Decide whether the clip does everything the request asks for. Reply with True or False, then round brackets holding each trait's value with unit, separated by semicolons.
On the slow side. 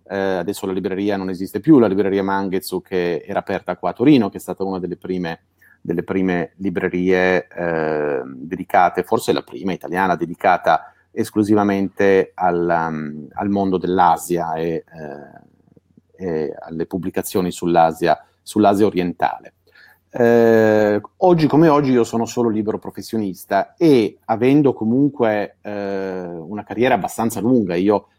False (135 wpm)